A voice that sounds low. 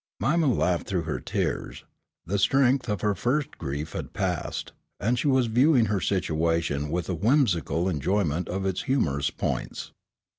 Yes: very low, 95 Hz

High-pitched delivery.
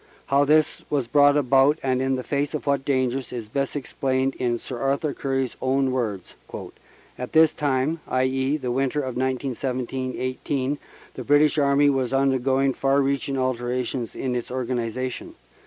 No: low, 135 Hz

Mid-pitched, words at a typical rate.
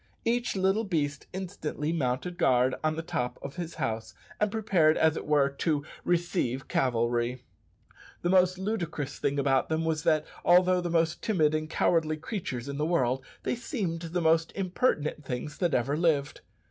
Yes: medium, 160 Hz; average, 170 wpm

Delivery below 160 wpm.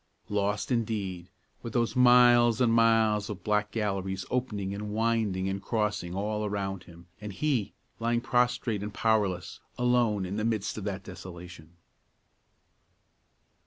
Yes: slow, 135 wpm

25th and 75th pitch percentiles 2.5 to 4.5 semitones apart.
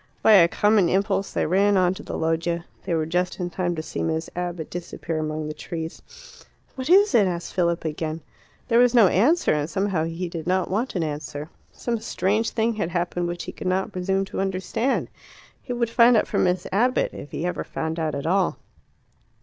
Yes: average, 3.9 semitones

